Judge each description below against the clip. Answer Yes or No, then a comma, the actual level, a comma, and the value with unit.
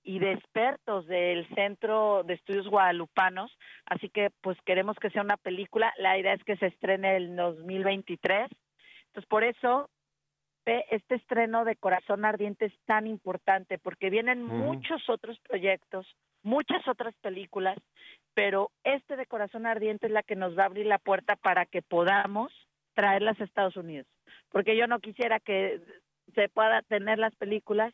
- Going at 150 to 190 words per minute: Yes, average, 160 wpm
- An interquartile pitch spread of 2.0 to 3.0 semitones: Yes, average, 2.7 semitones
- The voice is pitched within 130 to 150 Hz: No, high, 205 Hz